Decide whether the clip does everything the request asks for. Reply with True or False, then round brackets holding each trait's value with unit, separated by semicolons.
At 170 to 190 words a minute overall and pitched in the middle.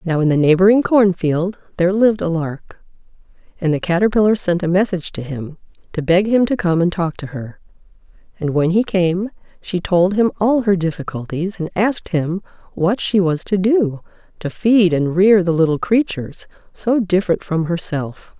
True (185 wpm; 180 Hz)